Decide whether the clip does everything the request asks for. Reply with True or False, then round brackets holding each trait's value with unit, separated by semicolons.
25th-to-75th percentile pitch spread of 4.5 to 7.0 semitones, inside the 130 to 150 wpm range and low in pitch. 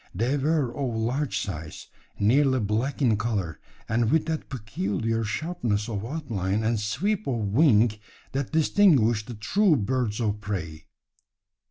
True (5.0 semitones; 140 wpm; 115 Hz)